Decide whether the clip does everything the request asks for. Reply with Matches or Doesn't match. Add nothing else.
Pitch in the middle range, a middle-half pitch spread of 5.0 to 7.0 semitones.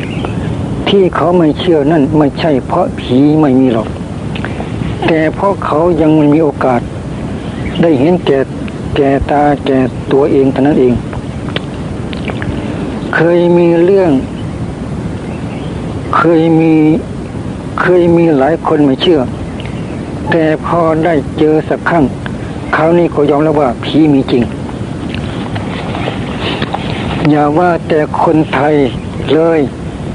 Doesn't match